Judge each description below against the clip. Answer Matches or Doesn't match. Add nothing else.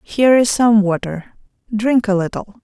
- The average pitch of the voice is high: Matches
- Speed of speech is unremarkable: Matches